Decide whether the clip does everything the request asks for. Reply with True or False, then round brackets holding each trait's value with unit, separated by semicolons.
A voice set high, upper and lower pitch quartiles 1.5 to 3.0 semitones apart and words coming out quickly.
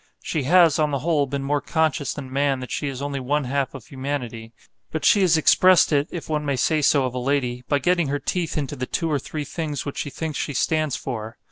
False (145 Hz; 2.6 semitones; 245 wpm)